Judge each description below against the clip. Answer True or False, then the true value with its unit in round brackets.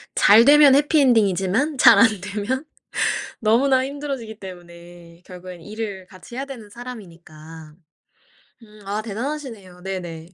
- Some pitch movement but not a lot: False (6.4 semitones)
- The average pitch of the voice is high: True (210 Hz)